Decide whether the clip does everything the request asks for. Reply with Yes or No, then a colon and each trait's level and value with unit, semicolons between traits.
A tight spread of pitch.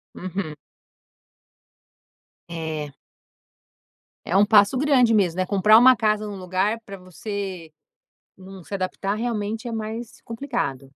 No: average, 3.4 semitones